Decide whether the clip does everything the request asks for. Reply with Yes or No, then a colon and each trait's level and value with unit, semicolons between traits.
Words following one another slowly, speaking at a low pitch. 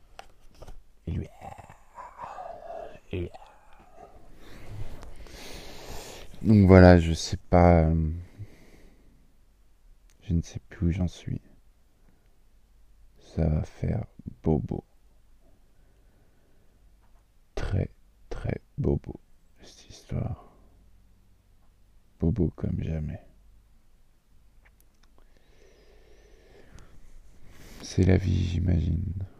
Yes: slow, 70 wpm; very low, 95 Hz